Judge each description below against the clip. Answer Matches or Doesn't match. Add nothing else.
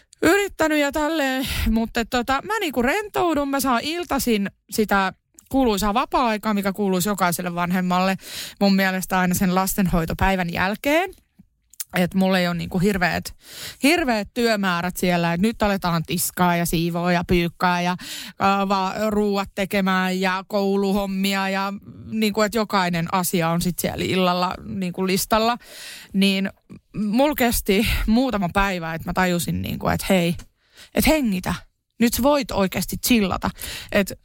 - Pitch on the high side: Matches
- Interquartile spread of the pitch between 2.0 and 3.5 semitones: Doesn't match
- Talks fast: Doesn't match